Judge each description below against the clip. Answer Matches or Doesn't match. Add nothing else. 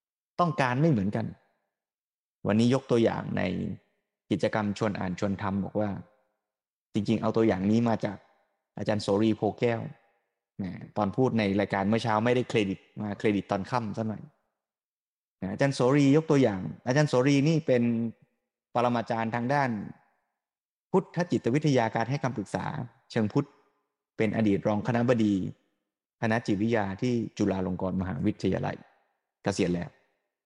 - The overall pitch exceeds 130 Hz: Doesn't match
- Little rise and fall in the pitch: Doesn't match